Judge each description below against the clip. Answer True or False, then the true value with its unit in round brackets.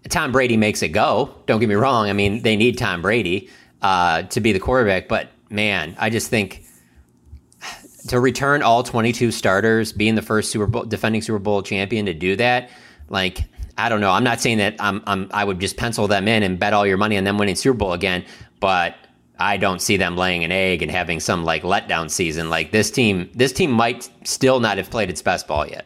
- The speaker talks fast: True (225 wpm)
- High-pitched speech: False (105 Hz)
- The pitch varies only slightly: False (3.3 semitones)